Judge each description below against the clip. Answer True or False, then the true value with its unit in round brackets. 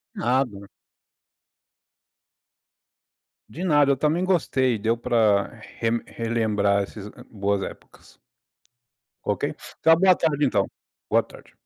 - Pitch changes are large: True (6.2 semitones)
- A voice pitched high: False (115 Hz)